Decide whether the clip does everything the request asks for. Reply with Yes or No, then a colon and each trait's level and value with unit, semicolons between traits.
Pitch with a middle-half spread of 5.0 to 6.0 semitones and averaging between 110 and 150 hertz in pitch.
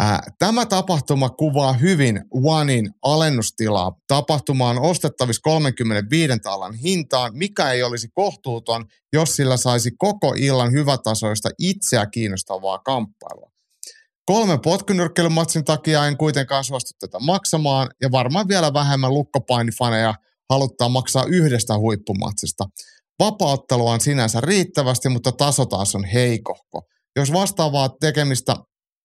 Yes: average, 5.3 semitones; low, 135 Hz